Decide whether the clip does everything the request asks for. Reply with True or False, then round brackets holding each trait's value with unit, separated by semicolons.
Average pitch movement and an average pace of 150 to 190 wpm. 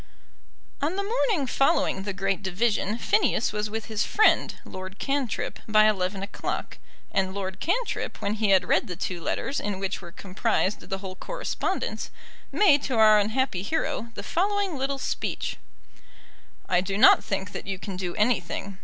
False (5.7 semitones; 165 wpm)